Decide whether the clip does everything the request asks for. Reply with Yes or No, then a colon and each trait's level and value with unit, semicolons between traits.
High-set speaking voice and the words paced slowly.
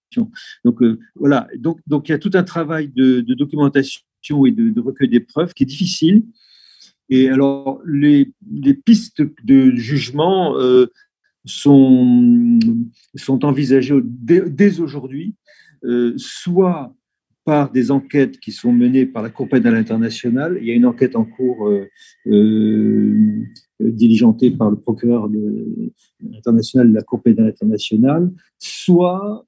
No: medium, 140 Hz; slow, 140 wpm